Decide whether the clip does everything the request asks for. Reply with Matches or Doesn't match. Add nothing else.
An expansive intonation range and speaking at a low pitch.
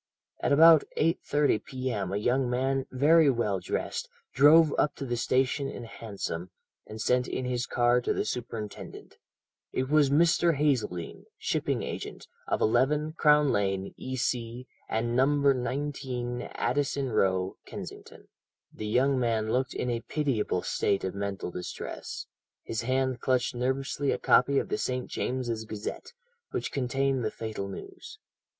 Doesn't match